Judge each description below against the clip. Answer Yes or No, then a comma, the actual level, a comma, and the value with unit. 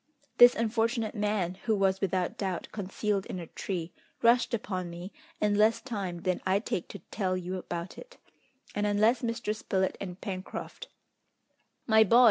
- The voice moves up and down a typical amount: Yes, average, 3.2 semitones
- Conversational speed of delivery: Yes, average, 165 wpm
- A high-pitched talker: Yes, high, 200 Hz